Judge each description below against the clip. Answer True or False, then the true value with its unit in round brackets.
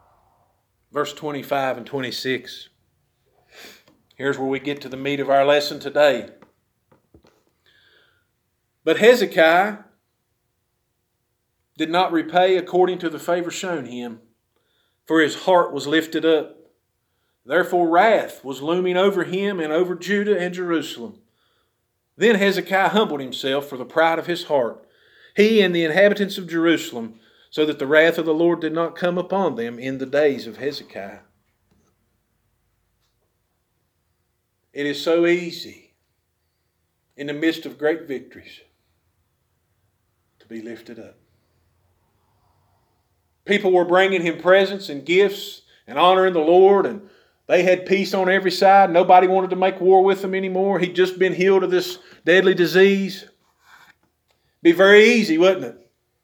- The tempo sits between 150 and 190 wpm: False (140 wpm)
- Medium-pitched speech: True (160 Hz)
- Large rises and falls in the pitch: True (7.5 semitones)